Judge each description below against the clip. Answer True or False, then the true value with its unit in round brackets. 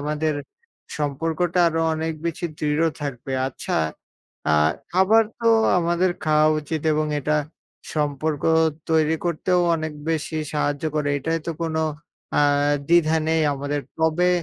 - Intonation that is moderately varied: False (1.8 semitones)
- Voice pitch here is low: False (160 Hz)